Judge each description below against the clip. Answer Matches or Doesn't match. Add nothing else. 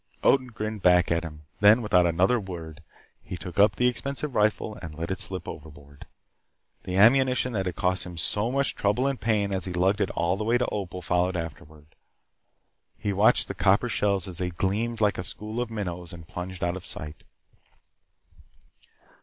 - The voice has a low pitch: Matches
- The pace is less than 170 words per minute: Doesn't match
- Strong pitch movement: Doesn't match